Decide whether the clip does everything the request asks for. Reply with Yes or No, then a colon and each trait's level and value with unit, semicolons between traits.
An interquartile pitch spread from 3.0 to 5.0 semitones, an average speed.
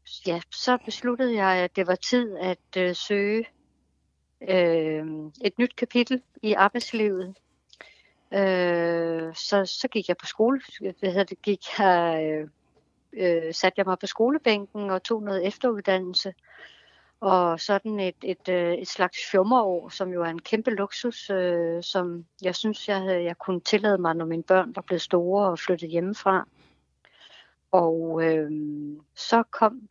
No: average, 3.4 semitones; slow, 140 wpm